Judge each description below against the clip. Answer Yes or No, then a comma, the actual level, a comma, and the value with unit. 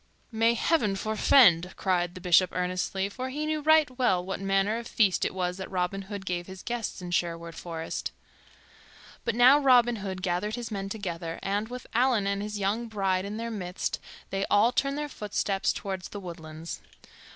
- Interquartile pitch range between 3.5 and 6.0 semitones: Yes, average, 4.2 semitones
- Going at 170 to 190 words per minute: Yes, average, 185 wpm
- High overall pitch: Yes, high, 195 Hz